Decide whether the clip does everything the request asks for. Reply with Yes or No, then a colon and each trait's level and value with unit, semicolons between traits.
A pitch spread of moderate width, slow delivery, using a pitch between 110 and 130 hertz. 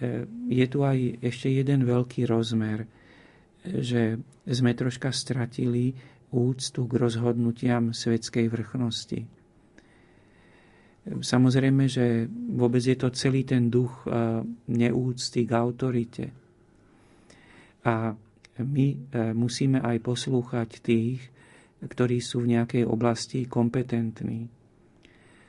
No: narrow, 1.6 semitones; slow, 90 wpm; low, 120 Hz